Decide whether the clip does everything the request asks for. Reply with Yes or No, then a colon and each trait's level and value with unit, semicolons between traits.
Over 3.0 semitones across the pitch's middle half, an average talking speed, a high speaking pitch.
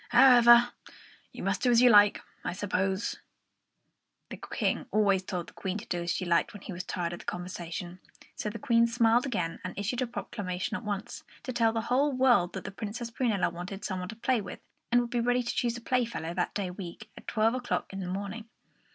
No: average, 4.6 semitones; fast, 220 wpm; high, 210 Hz